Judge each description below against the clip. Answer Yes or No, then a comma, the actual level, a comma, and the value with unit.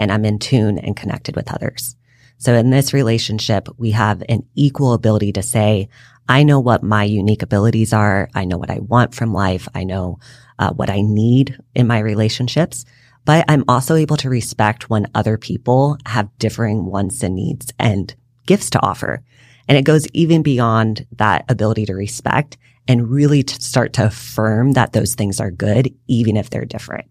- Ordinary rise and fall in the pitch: Yes, average, 3.4 semitones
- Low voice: Yes, low, 115 Hz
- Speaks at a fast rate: No, average, 185 wpm